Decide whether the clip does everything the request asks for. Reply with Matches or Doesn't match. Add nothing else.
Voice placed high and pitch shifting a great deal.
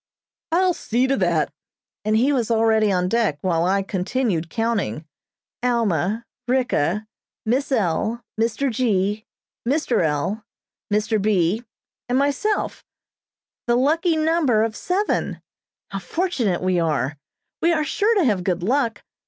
Matches